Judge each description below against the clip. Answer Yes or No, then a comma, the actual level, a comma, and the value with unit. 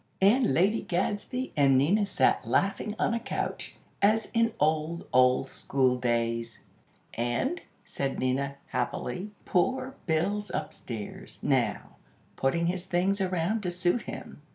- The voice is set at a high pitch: No, medium, 175 Hz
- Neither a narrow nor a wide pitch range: No, wide, 7.9 semitones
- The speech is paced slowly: Yes, slow, 130 wpm